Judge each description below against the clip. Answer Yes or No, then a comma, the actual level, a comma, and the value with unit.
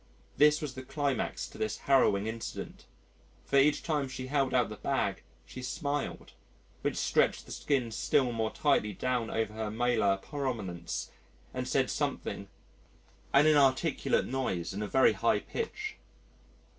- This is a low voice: Yes, low, 130 Hz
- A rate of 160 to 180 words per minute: No, average, 145 wpm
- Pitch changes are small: No, average, 4.3 semitones